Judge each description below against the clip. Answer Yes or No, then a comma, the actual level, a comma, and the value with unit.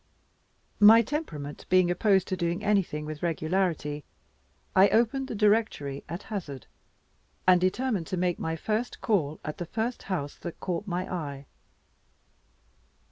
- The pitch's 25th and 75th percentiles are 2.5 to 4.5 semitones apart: No, average, 5.1 semitones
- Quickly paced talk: No, slow, 135 wpm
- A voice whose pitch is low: No, medium, 180 Hz